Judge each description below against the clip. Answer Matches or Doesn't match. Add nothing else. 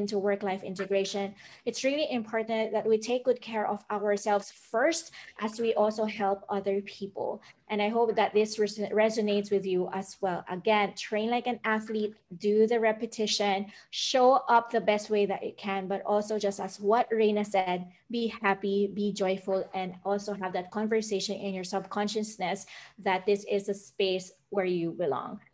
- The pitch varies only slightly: Matches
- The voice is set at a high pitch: Matches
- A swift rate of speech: Doesn't match